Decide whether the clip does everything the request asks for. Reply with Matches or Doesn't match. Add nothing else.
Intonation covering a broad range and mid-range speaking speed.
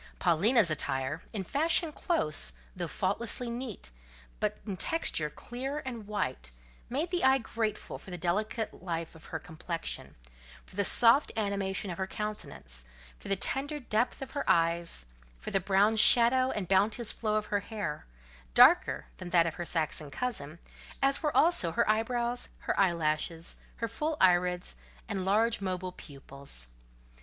Matches